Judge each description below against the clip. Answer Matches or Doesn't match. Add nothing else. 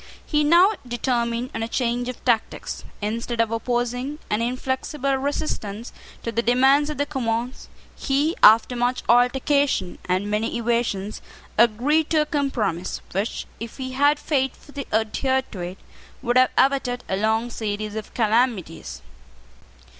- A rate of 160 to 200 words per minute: Doesn't match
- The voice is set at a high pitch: Matches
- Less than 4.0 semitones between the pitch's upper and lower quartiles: Matches